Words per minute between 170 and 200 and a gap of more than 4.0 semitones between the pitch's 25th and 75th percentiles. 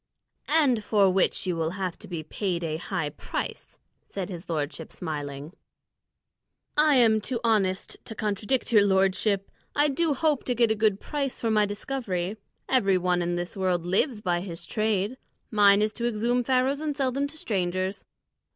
Yes: average, 175 wpm; average, 5.3 semitones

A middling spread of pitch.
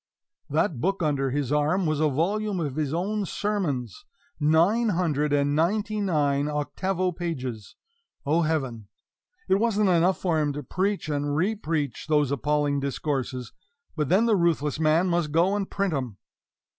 Yes: average, 4.5 semitones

